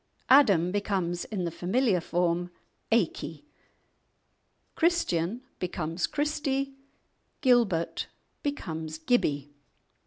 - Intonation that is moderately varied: No, wide, 7.3 semitones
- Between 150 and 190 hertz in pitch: Yes, medium, 185 Hz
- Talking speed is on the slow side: Yes, slow, 80 wpm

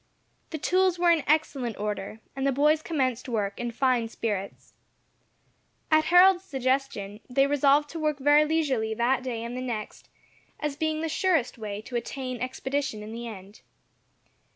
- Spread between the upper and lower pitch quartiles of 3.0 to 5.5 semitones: Yes, average, 4.9 semitones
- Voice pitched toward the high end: Yes, very high, 265 Hz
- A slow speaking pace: No, average, 160 wpm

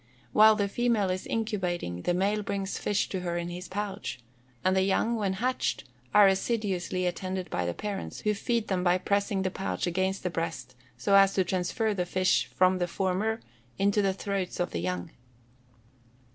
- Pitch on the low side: No, high, 190 Hz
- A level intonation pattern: Yes, narrow, 2.3 semitones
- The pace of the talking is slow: No, average, 185 wpm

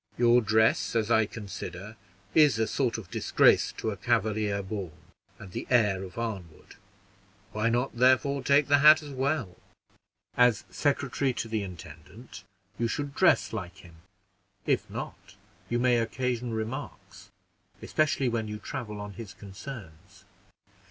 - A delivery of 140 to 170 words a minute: Yes, average, 145 wpm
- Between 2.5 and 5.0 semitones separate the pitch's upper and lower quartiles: Yes, average, 3.8 semitones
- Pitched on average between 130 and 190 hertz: No, low, 115 Hz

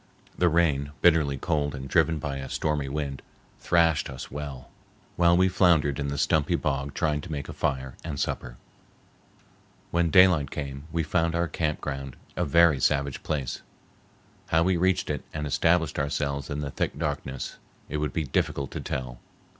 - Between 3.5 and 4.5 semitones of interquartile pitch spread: No, average, 3.1 semitones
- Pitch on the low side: Yes, very low, 75 Hz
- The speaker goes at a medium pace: Yes, average, 170 wpm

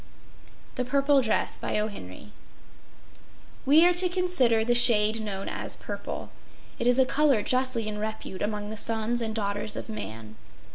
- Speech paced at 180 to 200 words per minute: No, average, 145 wpm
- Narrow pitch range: No, average, 3.7 semitones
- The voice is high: Yes, high, 225 Hz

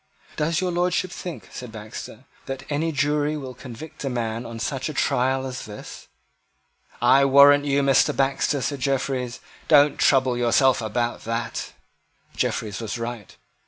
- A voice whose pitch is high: No, low, 135 Hz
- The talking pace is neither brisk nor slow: Yes, average, 150 wpm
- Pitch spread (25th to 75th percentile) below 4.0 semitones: Yes, average, 3.2 semitones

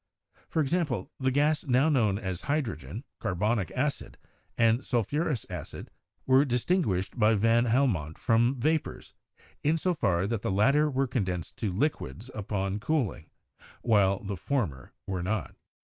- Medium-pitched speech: No, low, 115 Hz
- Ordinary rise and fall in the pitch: No, wide, 6.1 semitones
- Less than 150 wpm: Yes, average, 140 wpm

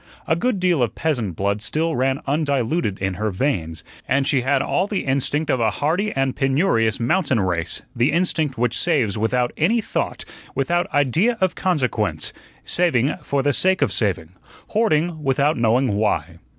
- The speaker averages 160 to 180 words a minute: Yes, average, 165 wpm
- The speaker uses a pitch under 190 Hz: Yes, low, 135 Hz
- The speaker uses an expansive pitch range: Yes, wide, 6.1 semitones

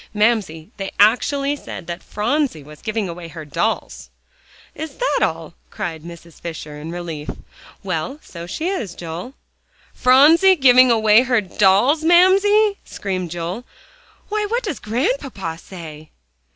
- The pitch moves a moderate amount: No, wide, 8.9 semitones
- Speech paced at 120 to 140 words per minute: Yes, slow, 135 wpm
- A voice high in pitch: Yes, high, 210 Hz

